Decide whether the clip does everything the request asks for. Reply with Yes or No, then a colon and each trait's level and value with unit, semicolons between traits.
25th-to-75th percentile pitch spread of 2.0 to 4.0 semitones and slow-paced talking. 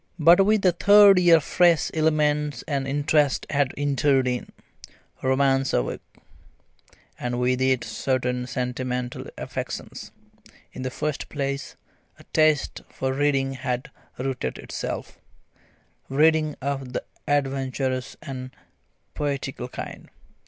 Yes: narrow, 2.5 semitones; slow, 110 wpm